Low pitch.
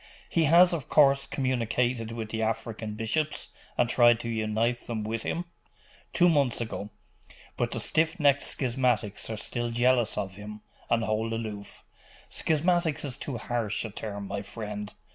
Yes: low, 115 Hz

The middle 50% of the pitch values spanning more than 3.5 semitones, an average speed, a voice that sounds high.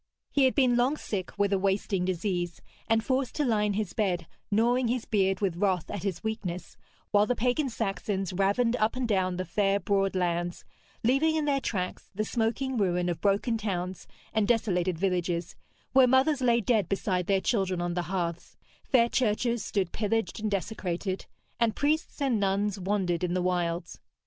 Yes: average, 4.2 semitones; average, 180 wpm; high, 200 Hz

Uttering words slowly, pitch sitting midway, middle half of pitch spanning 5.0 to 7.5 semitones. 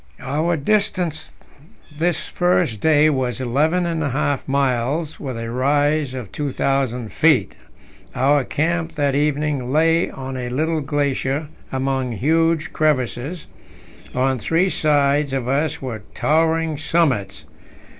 No: slow, 125 wpm; medium, 145 Hz; average, 3.4 semitones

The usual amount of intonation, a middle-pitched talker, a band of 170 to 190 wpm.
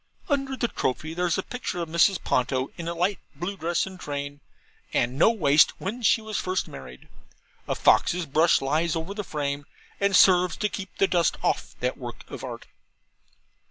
Yes: average, 5.0 semitones; medium, 170 Hz; average, 185 wpm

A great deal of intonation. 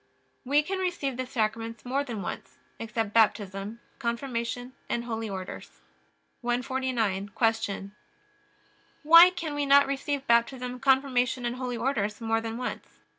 No: average, 3.2 semitones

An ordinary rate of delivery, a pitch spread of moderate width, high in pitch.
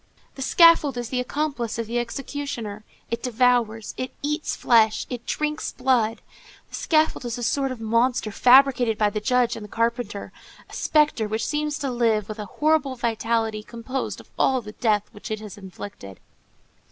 Yes: average, 175 wpm; average, 3.5 semitones; high, 240 Hz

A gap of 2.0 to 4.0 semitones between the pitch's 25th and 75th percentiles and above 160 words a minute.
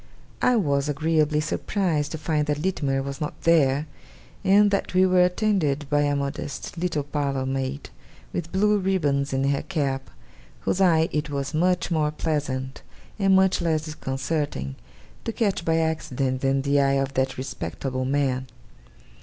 No: average, 3.7 semitones; average, 155 wpm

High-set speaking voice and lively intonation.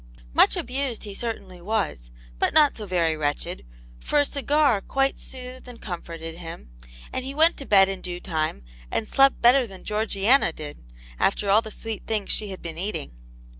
Yes: high, 210 Hz; wide, 6.4 semitones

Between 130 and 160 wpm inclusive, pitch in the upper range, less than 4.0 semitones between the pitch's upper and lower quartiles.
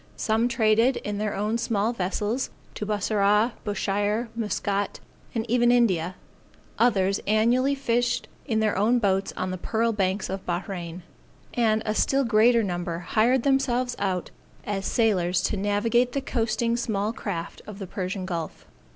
Yes: average, 150 wpm; high, 215 Hz; average, 3.2 semitones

